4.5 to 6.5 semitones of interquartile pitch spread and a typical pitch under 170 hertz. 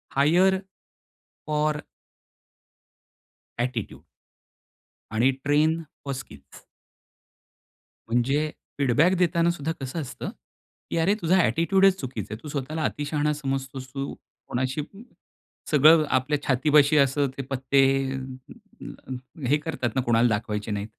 No: average, 3.2 semitones; medium, 140 Hz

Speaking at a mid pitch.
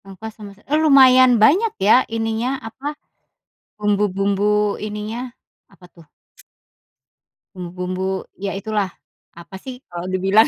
No: high, 210 Hz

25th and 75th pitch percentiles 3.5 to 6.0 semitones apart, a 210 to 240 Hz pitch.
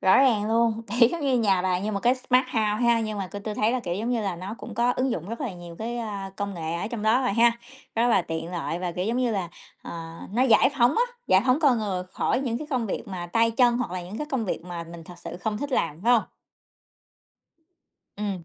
Yes: average, 4.7 semitones; high, 215 Hz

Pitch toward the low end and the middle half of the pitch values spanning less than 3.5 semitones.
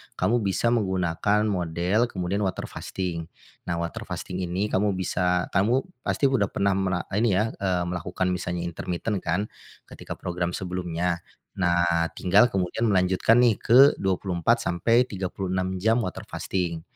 Yes: very low, 95 Hz; average, 2.8 semitones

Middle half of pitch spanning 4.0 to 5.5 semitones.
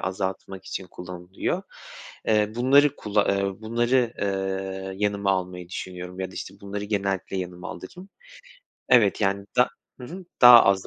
No: average, 2.7 semitones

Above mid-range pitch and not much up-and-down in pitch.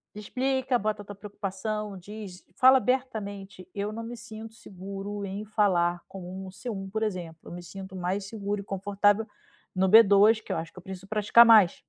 Yes: high, 200 Hz; narrow, 2.3 semitones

